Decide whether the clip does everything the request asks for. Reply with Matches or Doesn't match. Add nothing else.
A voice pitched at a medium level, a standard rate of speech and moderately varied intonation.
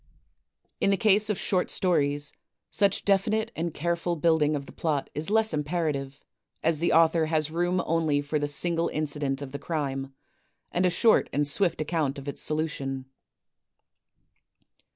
Matches